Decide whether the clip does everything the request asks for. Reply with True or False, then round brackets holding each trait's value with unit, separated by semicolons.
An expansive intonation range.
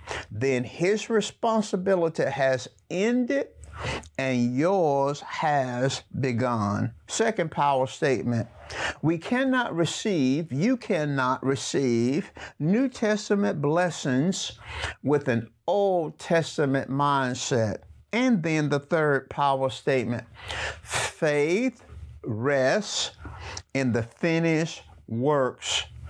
True (5.8 semitones)